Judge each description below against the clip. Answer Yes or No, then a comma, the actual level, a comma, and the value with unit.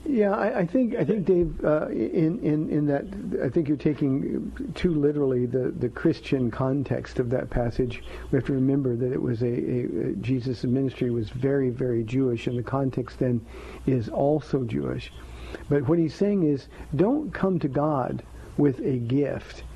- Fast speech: No, average, 180 wpm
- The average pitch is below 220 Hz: Yes, low, 135 Hz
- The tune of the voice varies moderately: Yes, average, 3.9 semitones